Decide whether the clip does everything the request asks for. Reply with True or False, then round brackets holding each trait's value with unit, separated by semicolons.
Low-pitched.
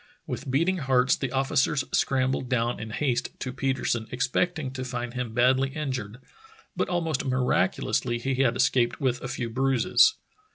True (130 Hz)